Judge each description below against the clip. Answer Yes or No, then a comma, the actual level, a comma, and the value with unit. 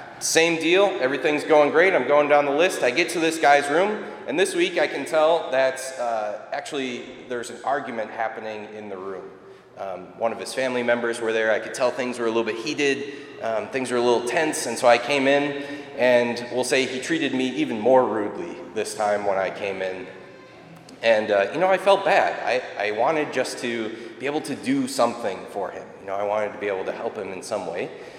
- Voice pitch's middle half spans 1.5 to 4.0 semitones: No, average, 4.8 semitones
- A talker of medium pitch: No, low, 130 Hz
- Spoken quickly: Yes, fast, 230 wpm